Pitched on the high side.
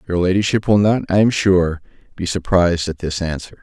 No: very low, 90 Hz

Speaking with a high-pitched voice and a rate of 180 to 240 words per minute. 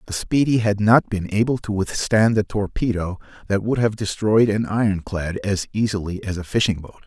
No: low, 105 Hz; average, 185 wpm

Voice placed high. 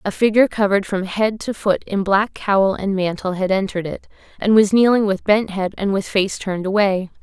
Yes: high, 200 Hz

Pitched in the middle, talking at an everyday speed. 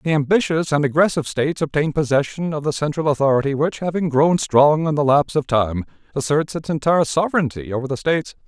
Yes: medium, 150 Hz; average, 190 wpm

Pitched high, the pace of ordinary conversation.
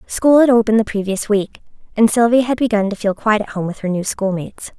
No: high, 215 Hz; fast, 240 wpm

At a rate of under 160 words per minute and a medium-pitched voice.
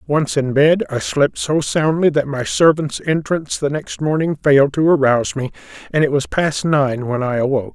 No: average, 200 wpm; medium, 145 Hz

